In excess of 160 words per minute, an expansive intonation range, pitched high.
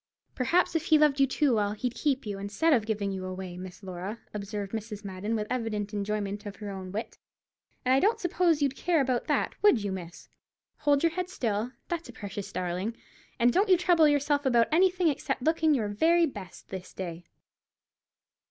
Yes: average, 195 wpm; wide, 7.1 semitones; high, 230 Hz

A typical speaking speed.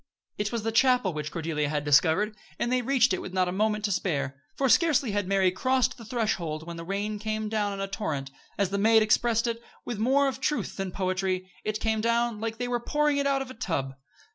No: fast, 235 wpm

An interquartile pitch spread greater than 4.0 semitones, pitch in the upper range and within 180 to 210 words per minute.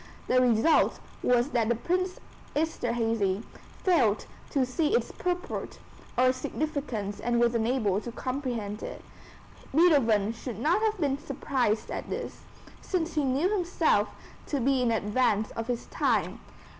No: average, 5.1 semitones; very high, 250 Hz; slow, 135 wpm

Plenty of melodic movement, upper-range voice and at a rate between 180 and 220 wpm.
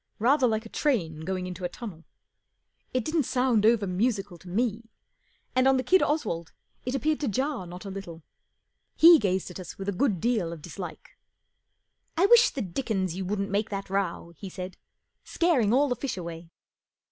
Yes: wide, 5.9 semitones; high, 205 Hz; average, 195 wpm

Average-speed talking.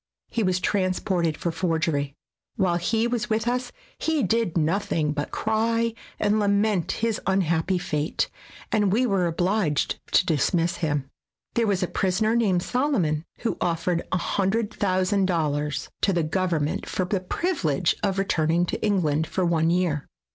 Yes: average, 155 wpm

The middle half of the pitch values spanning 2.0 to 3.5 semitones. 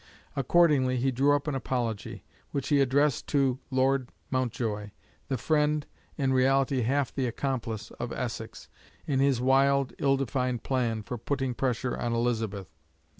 Yes: narrow, 2.4 semitones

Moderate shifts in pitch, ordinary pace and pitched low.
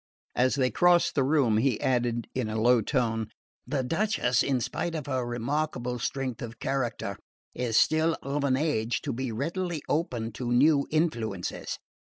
Yes: average, 3.9 semitones; average, 160 wpm; low, 130 Hz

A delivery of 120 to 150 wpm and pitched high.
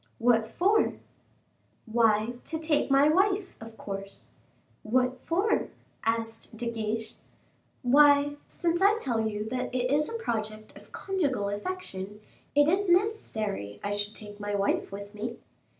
Yes: average, 140 wpm; high, 235 Hz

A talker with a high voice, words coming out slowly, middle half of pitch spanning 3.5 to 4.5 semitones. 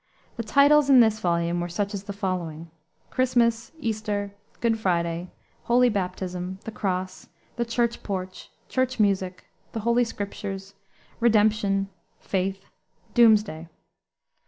Yes: high, 205 Hz; slow, 120 wpm; average, 3.9 semitones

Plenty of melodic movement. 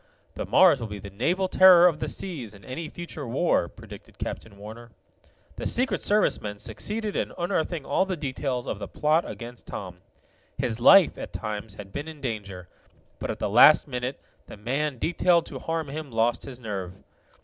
Yes: wide, 7.4 semitones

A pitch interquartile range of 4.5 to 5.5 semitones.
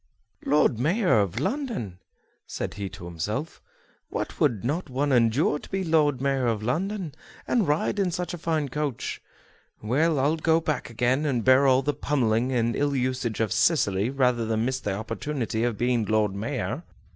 Yes: average, 5.0 semitones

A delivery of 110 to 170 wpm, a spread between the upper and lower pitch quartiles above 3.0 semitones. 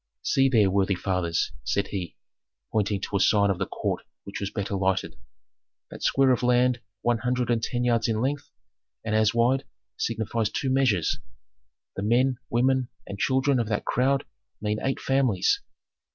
Yes: average, 165 wpm; average, 4.2 semitones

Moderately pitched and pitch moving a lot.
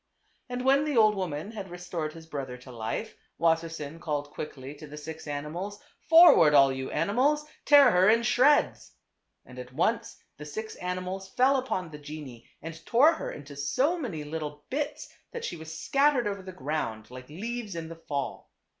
Yes: medium, 165 Hz; wide, 7.6 semitones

